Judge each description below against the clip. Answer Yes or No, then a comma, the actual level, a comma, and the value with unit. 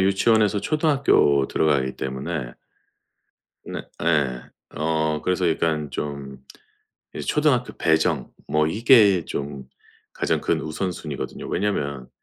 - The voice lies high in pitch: No, very low, 80 Hz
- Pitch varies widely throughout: Yes, wide, 5.7 semitones